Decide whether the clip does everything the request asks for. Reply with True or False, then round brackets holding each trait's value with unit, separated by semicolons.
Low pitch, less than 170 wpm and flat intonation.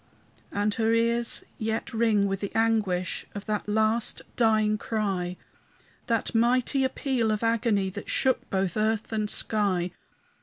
False (215 Hz; 140 wpm; 2.2 semitones)